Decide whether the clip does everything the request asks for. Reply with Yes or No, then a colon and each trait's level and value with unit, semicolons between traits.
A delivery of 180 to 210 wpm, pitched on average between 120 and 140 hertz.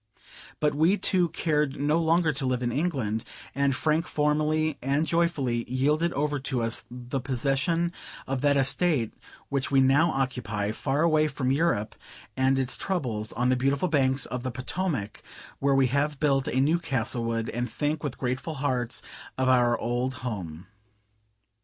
No: average, 160 wpm; low, 135 Hz